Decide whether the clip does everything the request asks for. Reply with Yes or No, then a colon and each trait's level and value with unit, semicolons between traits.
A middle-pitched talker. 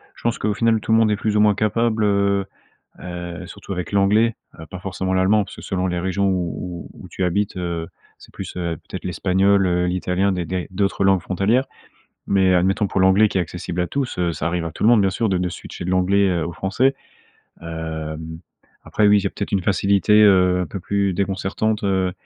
No: very low, 95 Hz